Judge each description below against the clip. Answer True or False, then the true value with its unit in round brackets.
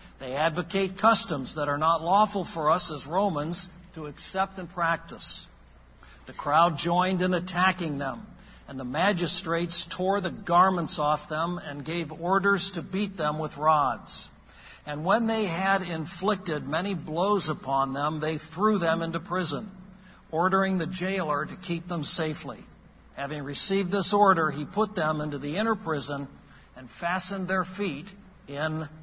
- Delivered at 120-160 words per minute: True (155 wpm)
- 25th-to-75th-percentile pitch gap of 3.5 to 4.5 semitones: True (3.9 semitones)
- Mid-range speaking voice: True (170 Hz)